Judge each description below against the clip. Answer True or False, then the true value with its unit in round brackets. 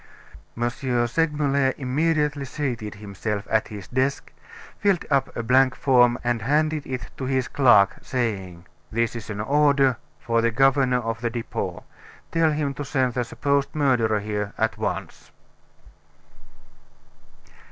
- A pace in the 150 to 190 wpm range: False (135 wpm)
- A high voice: False (125 Hz)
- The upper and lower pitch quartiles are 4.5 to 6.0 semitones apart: False (3.7 semitones)